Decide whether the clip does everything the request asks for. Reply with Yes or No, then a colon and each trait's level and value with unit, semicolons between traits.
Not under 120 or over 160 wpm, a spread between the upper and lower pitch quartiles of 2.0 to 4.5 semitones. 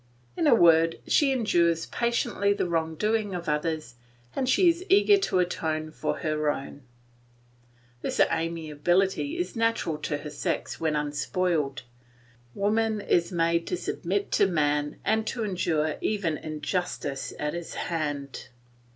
No: average, 140 wpm; average, 5.3 semitones